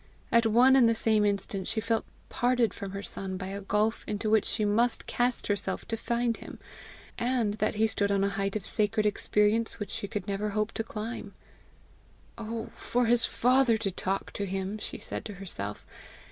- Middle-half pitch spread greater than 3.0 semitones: No, narrow, 2.5 semitones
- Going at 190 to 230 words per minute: Yes, average, 195 wpm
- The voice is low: No, high, 215 Hz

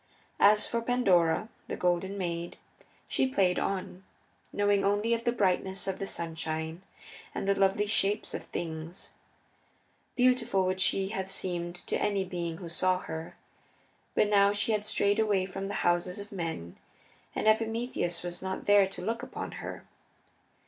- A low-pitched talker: No, high, 195 Hz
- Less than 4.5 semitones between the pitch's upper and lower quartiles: Yes, average, 2.8 semitones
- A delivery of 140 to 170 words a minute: Yes, average, 155 wpm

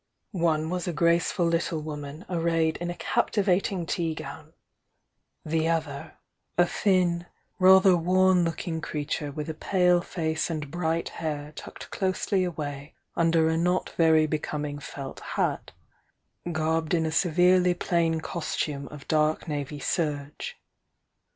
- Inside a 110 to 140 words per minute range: Yes, slow, 135 wpm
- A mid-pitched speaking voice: Yes, medium, 165 Hz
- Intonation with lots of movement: No, narrow, 2.4 semitones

